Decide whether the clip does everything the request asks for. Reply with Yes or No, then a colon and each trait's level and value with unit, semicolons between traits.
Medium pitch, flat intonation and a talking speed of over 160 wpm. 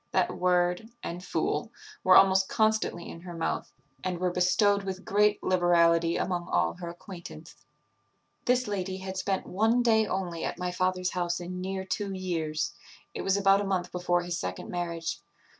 Yes: medium, 180 Hz; narrow, 1.9 semitones; average, 170 wpm